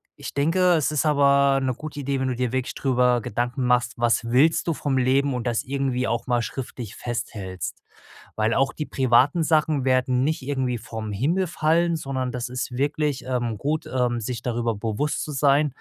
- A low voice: Yes, low, 130 Hz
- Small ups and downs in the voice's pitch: No, average, 3.0 semitones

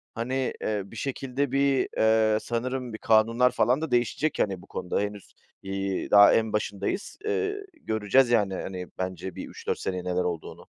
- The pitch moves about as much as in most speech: Yes, average, 4.6 semitones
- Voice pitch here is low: Yes, low, 110 Hz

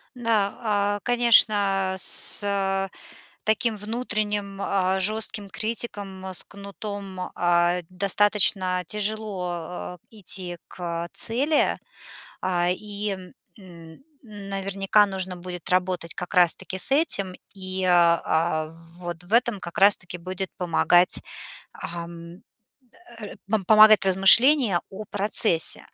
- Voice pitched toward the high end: Yes, high, 195 Hz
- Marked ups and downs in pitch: No, average, 2.7 semitones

